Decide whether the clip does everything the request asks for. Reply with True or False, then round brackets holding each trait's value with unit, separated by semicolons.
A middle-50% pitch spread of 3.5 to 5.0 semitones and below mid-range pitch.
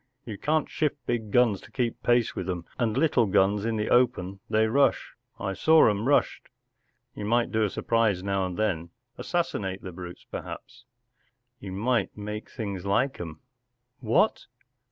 True (3.9 semitones; 110 Hz)